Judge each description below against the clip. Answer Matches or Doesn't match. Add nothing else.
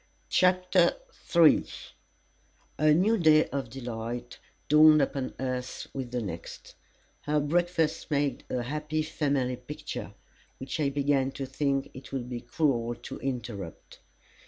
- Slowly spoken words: Matches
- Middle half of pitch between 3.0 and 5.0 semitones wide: Matches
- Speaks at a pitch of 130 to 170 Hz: Matches